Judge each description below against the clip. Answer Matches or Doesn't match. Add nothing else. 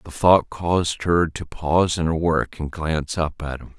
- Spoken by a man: Matches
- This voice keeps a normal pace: Doesn't match